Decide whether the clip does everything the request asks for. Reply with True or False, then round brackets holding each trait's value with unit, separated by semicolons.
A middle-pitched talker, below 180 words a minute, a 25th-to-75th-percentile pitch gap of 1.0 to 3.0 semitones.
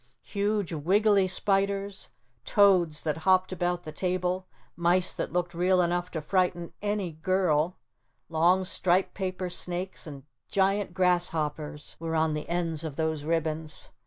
True (175 Hz; 135 wpm; 2.6 semitones)